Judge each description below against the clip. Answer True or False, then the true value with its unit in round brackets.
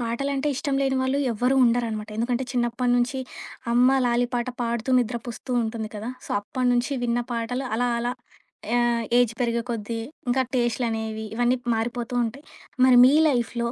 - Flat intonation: True (1.4 semitones)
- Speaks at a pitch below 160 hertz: False (240 Hz)